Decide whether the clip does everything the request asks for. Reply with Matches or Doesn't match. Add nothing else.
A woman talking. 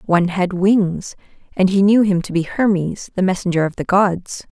Matches